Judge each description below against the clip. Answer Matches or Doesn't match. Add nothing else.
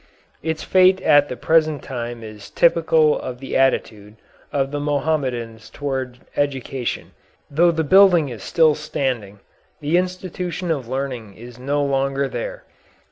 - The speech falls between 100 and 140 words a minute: Matches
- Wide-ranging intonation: Doesn't match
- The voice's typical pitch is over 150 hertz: Doesn't match